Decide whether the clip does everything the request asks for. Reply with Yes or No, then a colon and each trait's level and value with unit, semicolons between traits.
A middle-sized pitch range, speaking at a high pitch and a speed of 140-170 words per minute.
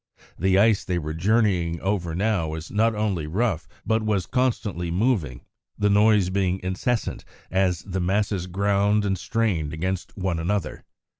No: average, 3.4 semitones; very low, 95 Hz; average, 150 wpm